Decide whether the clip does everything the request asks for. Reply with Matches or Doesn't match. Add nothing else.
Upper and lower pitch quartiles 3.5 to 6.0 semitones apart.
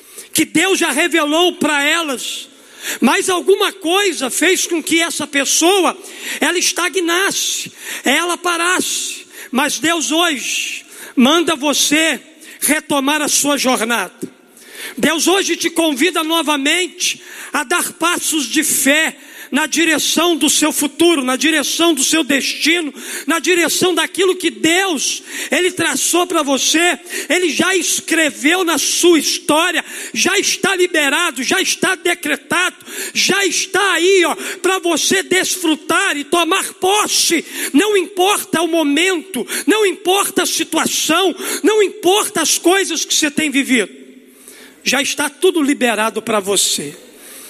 Doesn't match